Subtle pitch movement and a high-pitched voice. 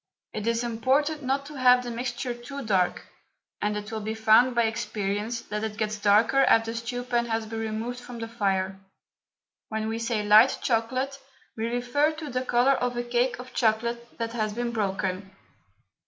Yes: narrow, 2.3 semitones; high, 230 Hz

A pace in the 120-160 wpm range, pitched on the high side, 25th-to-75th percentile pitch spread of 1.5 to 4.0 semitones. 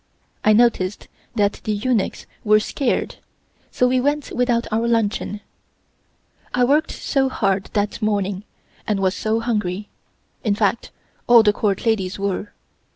Yes: average, 140 wpm; high, 215 Hz; average, 2.9 semitones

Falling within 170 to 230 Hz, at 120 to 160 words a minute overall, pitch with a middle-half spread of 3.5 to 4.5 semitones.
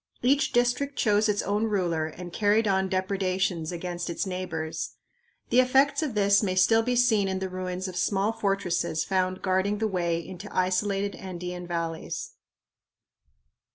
No: high, 190 Hz; average, 155 wpm; average, 2.7 semitones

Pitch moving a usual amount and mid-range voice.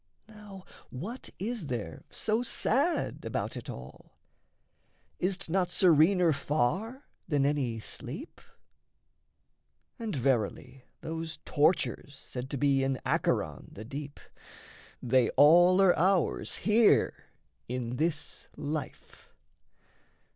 No: wide, 6.2 semitones; medium, 155 Hz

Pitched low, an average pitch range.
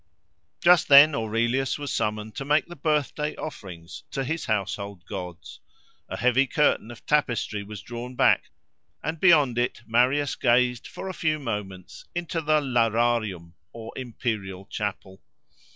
No: low, 120 Hz; wide, 5.7 semitones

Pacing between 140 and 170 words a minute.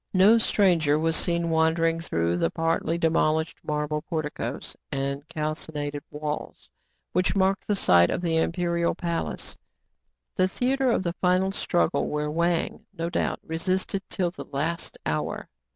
Yes: average, 145 wpm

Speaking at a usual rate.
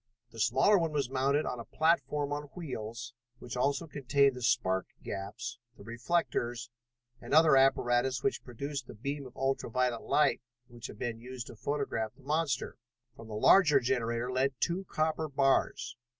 Yes: average, 165 wpm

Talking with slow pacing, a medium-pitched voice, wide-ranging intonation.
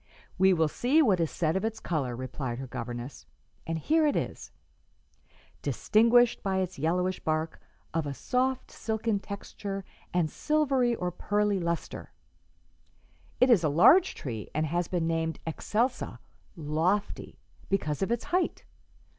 No: average, 145 wpm; medium, 180 Hz; wide, 6.1 semitones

